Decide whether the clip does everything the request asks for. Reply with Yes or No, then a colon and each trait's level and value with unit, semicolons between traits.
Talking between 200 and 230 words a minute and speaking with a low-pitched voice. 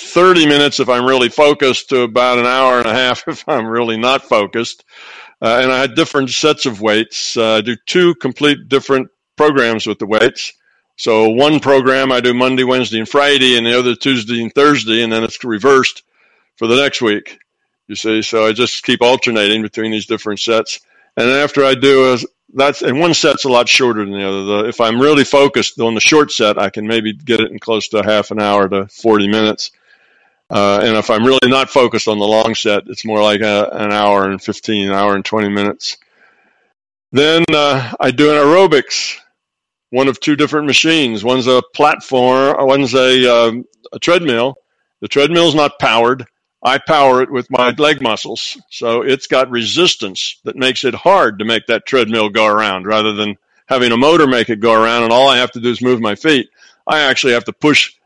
Yes: fast, 205 wpm; low, 125 Hz